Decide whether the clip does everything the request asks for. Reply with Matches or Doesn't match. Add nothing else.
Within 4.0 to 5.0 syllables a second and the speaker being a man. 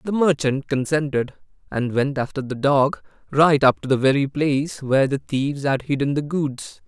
Matches